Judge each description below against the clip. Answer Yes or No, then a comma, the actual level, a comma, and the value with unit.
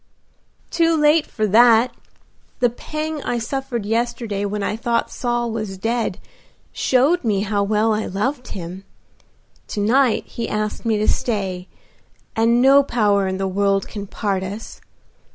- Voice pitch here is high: Yes, high, 225 Hz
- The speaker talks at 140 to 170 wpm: Yes, average, 150 wpm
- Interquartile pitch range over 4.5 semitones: No, average, 3.3 semitones